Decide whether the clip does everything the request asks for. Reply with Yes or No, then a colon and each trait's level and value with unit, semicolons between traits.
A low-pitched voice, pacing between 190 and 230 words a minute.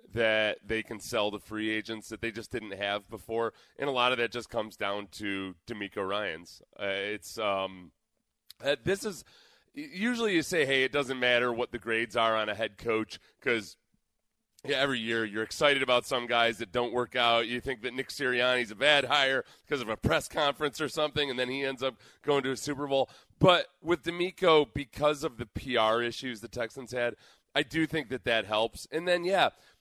Yes: low, 125 Hz; fast, 205 wpm